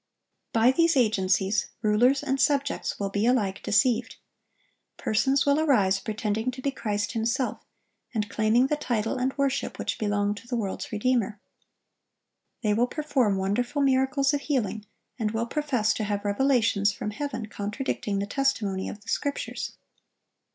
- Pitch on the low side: No, high, 230 Hz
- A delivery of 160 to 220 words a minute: No, average, 150 wpm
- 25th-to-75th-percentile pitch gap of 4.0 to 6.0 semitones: Yes, average, 4.5 semitones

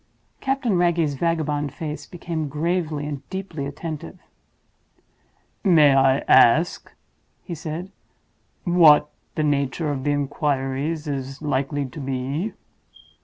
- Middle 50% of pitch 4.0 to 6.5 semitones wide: No, average, 3.1 semitones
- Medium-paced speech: No, slow, 110 wpm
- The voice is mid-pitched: Yes, medium, 150 Hz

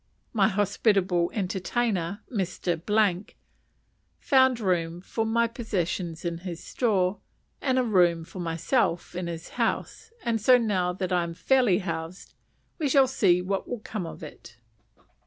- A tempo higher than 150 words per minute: No, average, 140 wpm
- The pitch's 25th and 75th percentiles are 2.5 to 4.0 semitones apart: No, average, 4.7 semitones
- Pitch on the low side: No, high, 190 Hz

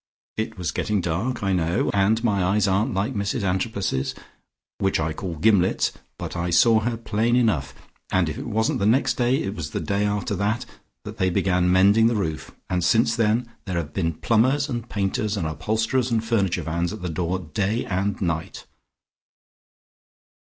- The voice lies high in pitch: No, low, 100 Hz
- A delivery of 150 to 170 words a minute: No, average, 180 wpm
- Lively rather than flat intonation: No, average, 3.9 semitones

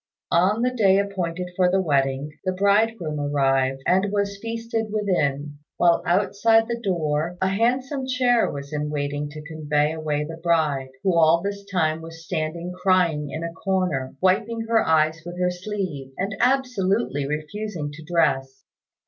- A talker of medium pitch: Yes, medium, 175 Hz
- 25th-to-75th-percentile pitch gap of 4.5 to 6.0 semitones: Yes, average, 5.0 semitones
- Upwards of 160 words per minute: No, average, 155 wpm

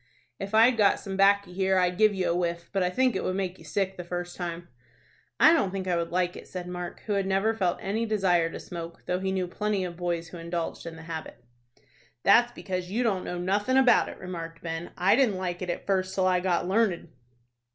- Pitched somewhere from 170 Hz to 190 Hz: Yes, medium, 185 Hz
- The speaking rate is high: Yes, fast, 235 wpm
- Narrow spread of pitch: Yes, narrow, 2.2 semitones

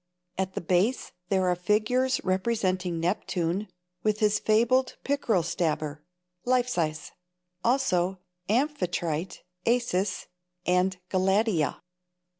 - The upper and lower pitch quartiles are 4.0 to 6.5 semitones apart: Yes, average, 4.5 semitones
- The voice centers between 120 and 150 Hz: No, high, 190 Hz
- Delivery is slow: Yes, slow, 95 wpm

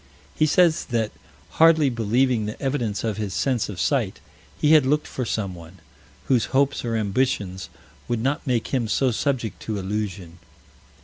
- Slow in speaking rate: No, average, 160 wpm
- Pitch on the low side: Yes, low, 115 Hz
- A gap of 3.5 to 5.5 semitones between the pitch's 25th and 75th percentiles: Yes, average, 4.4 semitones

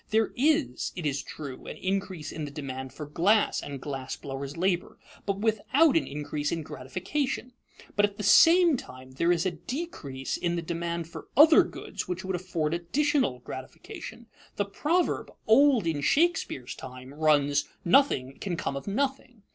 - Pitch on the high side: No, medium, 175 Hz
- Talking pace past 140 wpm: Yes, average, 165 wpm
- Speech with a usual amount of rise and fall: No, wide, 8.5 semitones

